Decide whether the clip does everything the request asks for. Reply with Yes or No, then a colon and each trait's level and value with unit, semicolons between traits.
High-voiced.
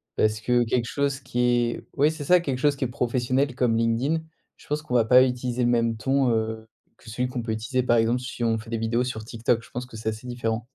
No: low, 120 Hz